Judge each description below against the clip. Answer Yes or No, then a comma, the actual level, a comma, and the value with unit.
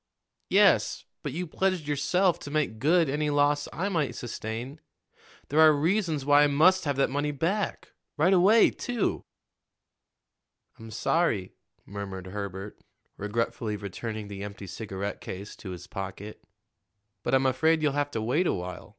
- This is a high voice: No, medium, 140 Hz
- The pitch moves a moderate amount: No, wide, 7.5 semitones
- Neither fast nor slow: Yes, average, 150 wpm